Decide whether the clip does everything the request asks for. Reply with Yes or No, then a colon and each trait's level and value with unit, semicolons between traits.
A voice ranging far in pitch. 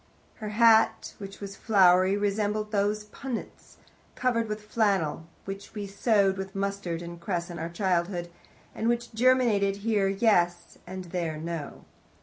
No: average, 3.3 semitones